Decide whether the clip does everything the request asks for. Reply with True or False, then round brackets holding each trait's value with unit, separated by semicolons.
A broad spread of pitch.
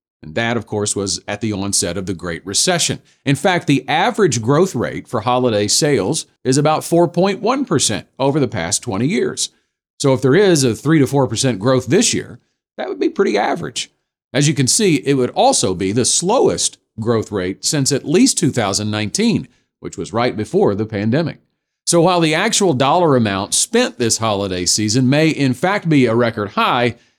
True (6.3 semitones)